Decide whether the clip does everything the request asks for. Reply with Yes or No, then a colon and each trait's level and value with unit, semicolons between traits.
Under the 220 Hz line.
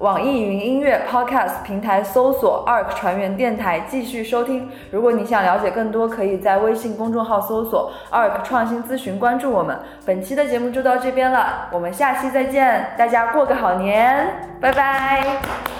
No: high, 240 Hz